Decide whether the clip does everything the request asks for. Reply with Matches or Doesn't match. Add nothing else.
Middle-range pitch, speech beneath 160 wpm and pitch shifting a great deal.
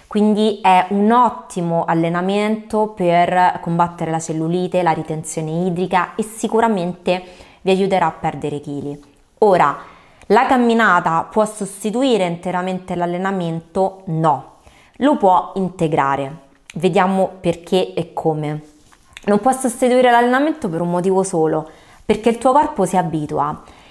Doesn't match